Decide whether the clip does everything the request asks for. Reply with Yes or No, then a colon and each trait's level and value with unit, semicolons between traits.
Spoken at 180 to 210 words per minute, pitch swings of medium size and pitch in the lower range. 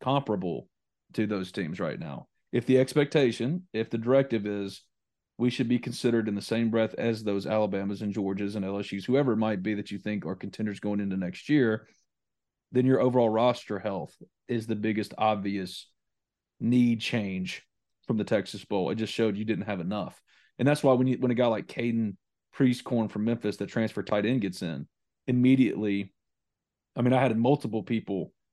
Yes: average, 185 wpm; average, 3.3 semitones; low, 110 Hz